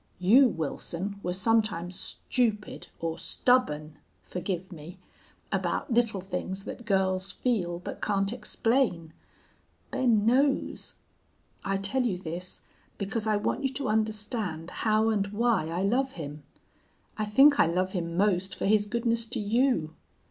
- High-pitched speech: Yes, high, 200 Hz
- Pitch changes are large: No, average, 4.3 semitones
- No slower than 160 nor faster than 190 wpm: No, average, 140 wpm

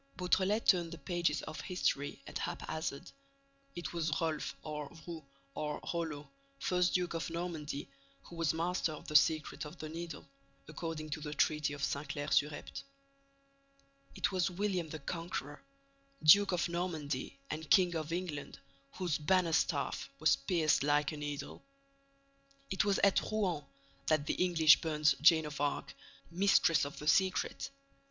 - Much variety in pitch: No, average, 2.9 semitones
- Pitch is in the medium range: Yes, medium, 160 Hz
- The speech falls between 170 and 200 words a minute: No, average, 150 wpm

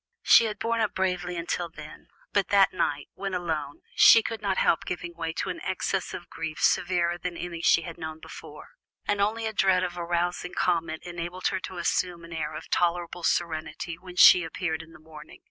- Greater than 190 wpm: Yes, average, 200 wpm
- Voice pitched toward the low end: No, medium, 175 Hz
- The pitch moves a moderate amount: No, narrow, 2.0 semitones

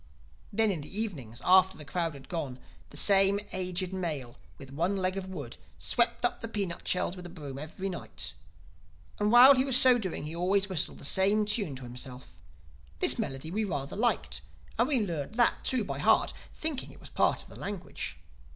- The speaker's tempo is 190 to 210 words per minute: Yes, average, 195 wpm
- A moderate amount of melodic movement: No, wide, 5.7 semitones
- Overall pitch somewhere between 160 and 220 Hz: Yes, medium, 185 Hz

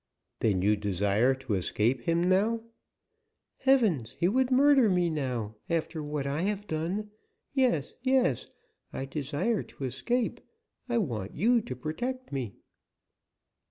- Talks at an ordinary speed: No, slow, 130 wpm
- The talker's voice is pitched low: No, medium, 160 Hz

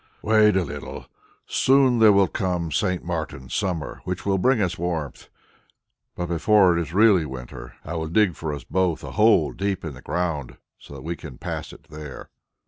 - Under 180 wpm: No, average, 185 wpm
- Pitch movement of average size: Yes, average, 4.0 semitones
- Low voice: Yes, very low, 85 Hz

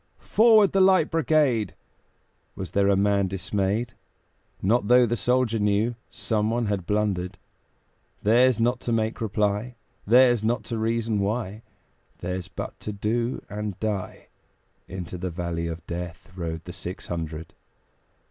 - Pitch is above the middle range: No, low, 105 Hz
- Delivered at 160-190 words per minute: No, average, 140 wpm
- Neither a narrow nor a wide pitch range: Yes, average, 4.2 semitones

